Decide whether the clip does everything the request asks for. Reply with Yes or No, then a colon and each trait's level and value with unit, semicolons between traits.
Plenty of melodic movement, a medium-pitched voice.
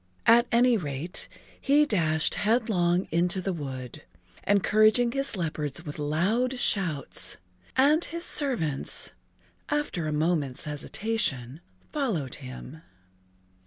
Yes: wide, 7.7 semitones; medium, 180 Hz